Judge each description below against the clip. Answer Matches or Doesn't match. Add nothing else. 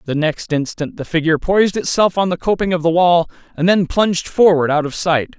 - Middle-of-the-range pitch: Matches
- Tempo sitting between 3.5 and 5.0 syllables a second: Doesn't match